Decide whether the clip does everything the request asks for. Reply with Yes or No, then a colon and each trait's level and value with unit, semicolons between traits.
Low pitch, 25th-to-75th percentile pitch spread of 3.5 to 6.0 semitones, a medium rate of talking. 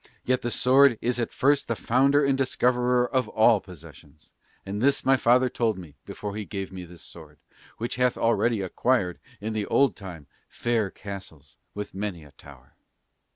Yes: low, 110 Hz; wide, 5.6 semitones; average, 175 wpm